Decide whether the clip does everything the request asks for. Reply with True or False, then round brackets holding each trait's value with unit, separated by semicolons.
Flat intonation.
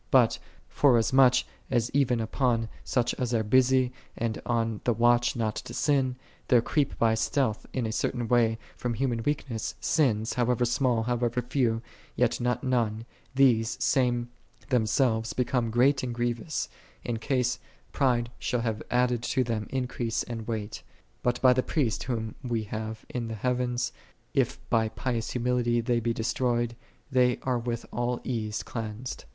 True (1.8 semitones)